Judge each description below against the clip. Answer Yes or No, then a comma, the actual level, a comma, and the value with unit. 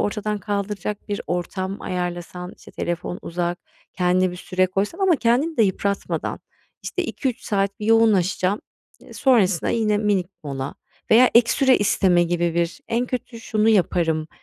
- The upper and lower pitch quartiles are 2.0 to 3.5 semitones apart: No, average, 4.0 semitones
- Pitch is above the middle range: Yes, high, 200 Hz